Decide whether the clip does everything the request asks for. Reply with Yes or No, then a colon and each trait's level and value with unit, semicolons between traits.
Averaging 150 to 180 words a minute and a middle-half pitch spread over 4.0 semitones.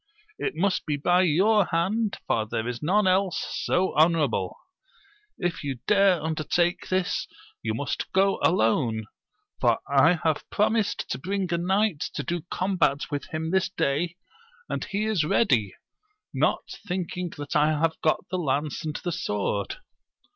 Yes: average, 155 wpm; average, 4.5 semitones